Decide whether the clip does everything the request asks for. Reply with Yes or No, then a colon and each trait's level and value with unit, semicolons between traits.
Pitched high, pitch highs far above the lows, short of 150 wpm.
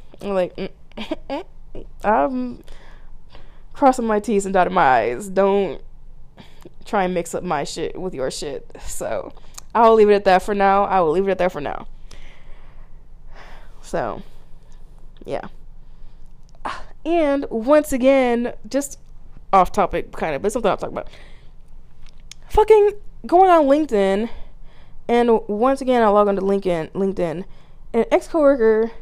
Yes: high, 220 Hz; wide, 6.0 semitones; average, 140 wpm